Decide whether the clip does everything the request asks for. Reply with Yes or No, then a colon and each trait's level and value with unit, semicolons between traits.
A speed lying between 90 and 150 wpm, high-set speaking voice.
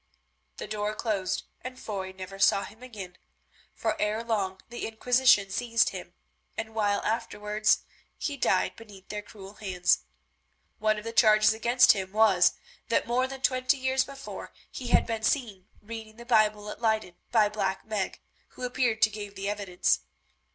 No: average, 165 wpm; high, 215 Hz